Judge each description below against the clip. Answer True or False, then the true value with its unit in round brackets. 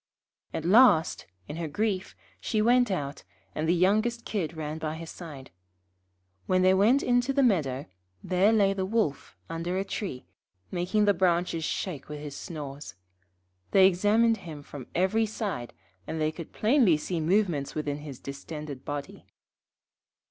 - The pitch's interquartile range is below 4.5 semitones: False (5.5 semitones)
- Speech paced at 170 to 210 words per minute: False (155 wpm)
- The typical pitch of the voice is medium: True (175 Hz)